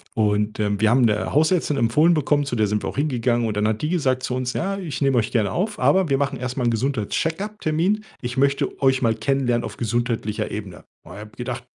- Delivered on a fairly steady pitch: No, average, 4.9 semitones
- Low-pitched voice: Yes, low, 125 Hz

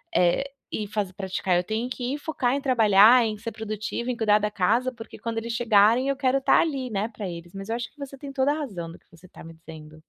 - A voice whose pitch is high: Yes, high, 220 Hz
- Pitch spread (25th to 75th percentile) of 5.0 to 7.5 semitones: No, average, 4.5 semitones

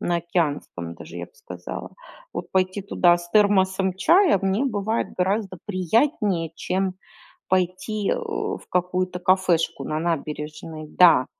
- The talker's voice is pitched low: No, medium, 185 Hz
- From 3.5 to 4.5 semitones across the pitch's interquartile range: No, average, 2.9 semitones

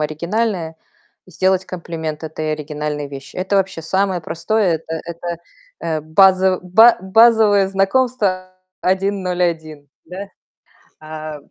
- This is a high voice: No, medium, 180 Hz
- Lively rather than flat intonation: No, average, 3.6 semitones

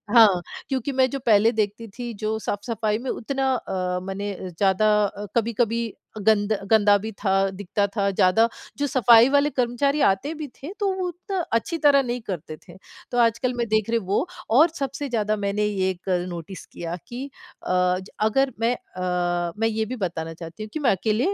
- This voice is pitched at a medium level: No, high, 220 Hz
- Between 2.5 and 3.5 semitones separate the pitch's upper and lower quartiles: No, average, 4.3 semitones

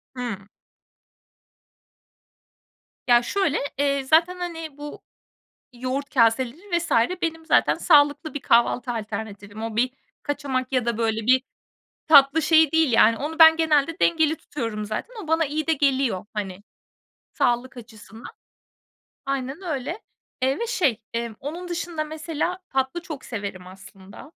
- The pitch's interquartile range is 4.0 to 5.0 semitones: No, wide, 5.6 semitones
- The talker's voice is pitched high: Yes, very high, 275 Hz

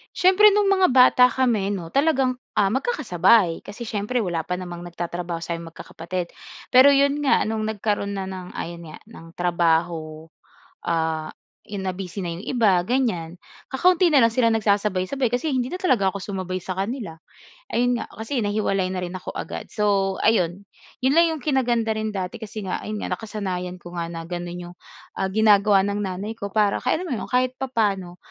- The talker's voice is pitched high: Yes, high, 200 Hz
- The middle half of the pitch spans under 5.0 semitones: No, wide, 5.5 semitones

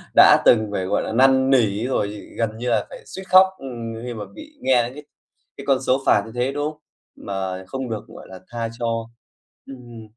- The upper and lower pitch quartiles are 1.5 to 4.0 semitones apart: Yes, average, 3.4 semitones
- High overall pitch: No, low, 120 Hz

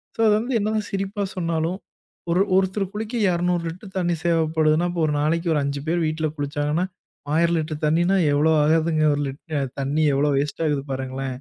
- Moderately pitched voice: Yes, medium, 165 Hz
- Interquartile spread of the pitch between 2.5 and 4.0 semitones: Yes, average, 3.3 semitones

